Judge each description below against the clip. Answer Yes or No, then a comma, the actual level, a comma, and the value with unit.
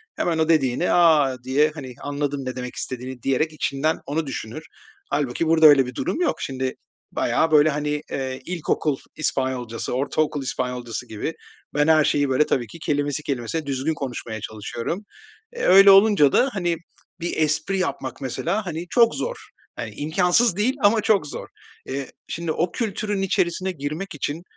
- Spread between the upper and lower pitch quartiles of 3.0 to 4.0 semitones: No, average, 4.5 semitones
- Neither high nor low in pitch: Yes, medium, 150 Hz